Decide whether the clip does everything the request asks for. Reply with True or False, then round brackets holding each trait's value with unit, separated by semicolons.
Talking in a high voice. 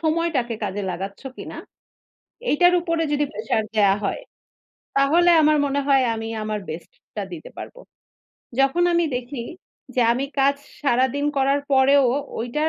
True (270 Hz)